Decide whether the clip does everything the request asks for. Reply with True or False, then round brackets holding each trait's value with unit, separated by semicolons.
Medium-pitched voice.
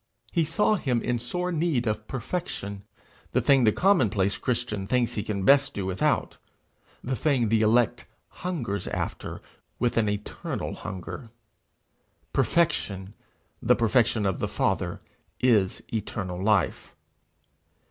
False (115 Hz)